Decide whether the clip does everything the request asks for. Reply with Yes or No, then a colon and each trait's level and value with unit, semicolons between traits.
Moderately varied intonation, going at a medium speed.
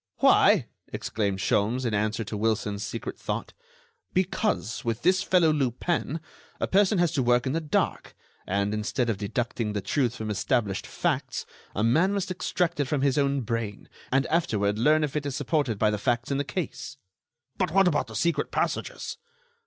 No: wide, 6.5 semitones; average, 180 wpm